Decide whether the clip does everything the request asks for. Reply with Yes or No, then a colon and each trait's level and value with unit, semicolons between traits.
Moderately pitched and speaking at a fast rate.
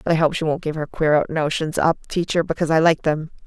Yes: medium, 160 Hz; fast, 260 wpm